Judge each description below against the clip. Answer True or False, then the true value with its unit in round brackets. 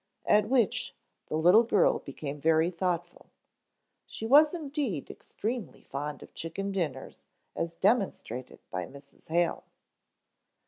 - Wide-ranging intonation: True (6.6 semitones)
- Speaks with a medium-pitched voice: True (175 Hz)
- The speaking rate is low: True (120 wpm)